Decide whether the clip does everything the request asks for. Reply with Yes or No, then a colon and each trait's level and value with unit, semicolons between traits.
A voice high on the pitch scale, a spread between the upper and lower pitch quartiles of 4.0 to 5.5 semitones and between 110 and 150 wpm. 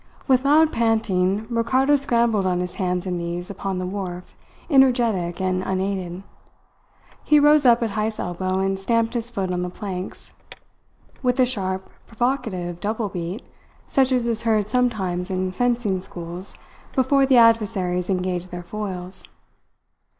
Yes: high, 200 Hz; average, 4.6 semitones; average, 145 wpm